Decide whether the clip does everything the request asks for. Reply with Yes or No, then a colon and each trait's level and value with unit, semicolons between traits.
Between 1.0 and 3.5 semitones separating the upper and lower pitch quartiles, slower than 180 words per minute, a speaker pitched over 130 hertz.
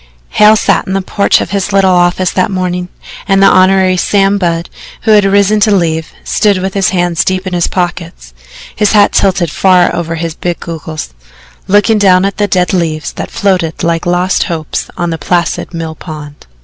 No: narrow, 2.6 semitones; average, 190 wpm; medium, 185 Hz